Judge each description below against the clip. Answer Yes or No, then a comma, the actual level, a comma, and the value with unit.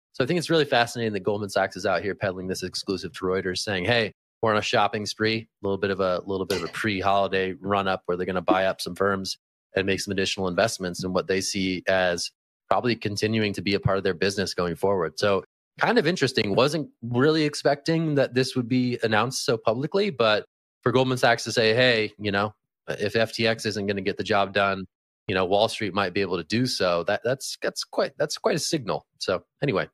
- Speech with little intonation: No, average, 3.5 semitones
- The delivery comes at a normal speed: No, fast, 225 wpm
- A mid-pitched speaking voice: No, low, 105 Hz